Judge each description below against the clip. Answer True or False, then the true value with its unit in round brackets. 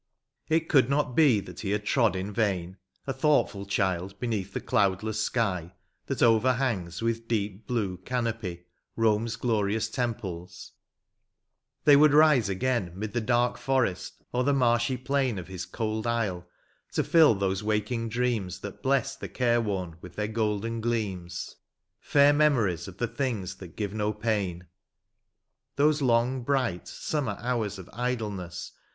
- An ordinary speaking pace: True (150 wpm)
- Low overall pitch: True (110 Hz)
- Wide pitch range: False (4.3 semitones)